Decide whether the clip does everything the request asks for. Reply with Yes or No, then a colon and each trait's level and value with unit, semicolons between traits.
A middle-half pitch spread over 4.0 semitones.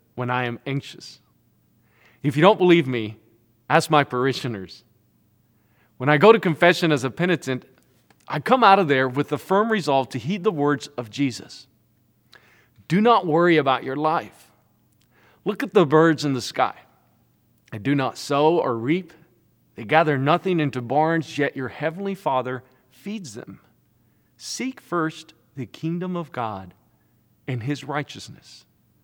Yes: average, 4.9 semitones